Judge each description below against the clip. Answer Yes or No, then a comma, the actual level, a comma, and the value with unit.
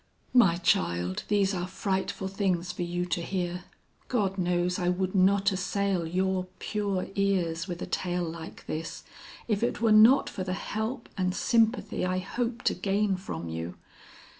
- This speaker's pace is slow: No, average, 165 wpm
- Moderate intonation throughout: No, narrow, 2.3 semitones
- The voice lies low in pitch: No, medium, 185 Hz